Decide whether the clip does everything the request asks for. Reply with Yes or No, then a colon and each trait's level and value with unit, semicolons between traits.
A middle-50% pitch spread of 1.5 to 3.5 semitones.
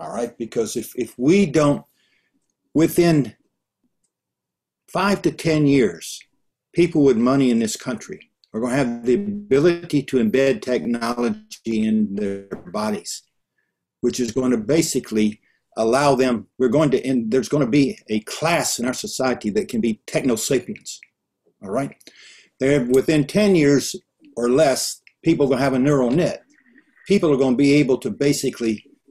No: average, 5.3 semitones